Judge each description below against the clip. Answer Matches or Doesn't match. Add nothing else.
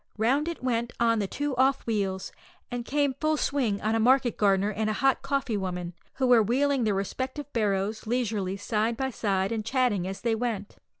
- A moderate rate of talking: Matches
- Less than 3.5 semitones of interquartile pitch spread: Doesn't match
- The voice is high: Matches